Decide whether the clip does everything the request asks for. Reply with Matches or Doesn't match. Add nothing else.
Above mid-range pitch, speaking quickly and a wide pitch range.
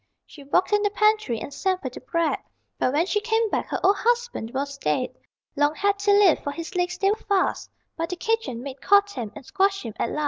Matches